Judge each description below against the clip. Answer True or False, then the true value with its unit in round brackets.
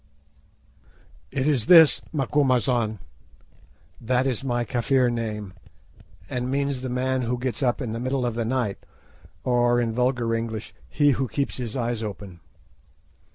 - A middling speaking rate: True (145 wpm)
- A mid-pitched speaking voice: False (125 Hz)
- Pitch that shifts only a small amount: True (2.3 semitones)